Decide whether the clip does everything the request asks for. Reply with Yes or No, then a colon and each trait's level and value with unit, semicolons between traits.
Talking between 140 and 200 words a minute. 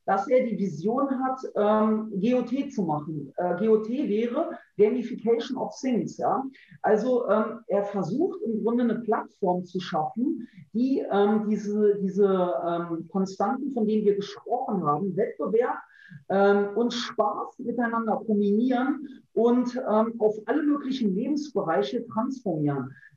No: average, 130 wpm